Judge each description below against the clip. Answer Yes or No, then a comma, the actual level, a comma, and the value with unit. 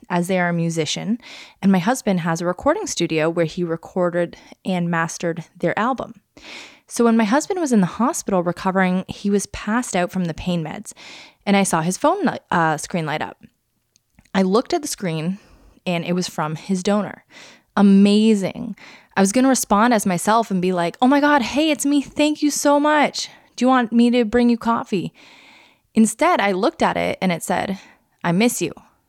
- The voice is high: Yes, high, 205 Hz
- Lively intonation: Yes, wide, 5.8 semitones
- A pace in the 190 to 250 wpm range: Yes, average, 200 wpm